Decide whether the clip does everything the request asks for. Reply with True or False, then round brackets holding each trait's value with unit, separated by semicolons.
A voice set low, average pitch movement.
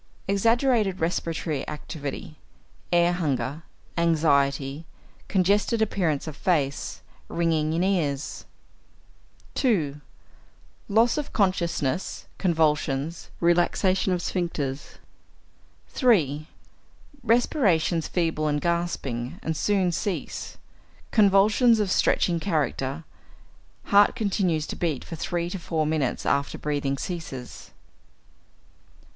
False (170 Hz; 4.4 semitones)